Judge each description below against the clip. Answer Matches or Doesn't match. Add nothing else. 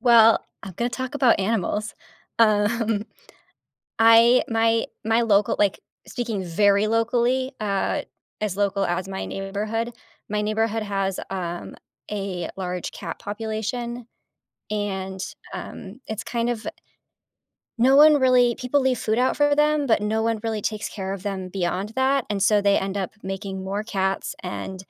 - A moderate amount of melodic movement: Matches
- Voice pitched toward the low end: Doesn't match